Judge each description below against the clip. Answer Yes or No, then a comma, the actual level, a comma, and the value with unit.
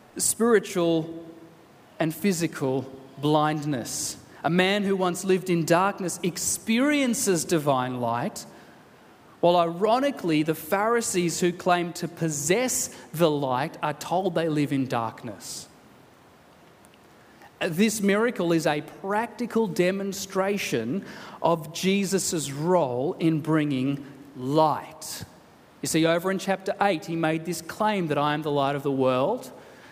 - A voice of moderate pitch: Yes, medium, 170 Hz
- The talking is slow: Yes, slow, 120 wpm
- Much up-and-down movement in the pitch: No, average, 4.3 semitones